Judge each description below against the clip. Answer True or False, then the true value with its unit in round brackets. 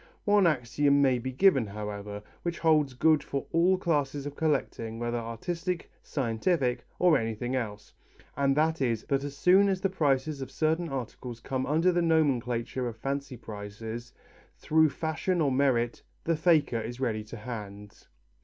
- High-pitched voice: False (135 Hz)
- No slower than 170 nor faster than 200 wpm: False (160 wpm)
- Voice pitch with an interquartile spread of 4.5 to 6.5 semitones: True (5.3 semitones)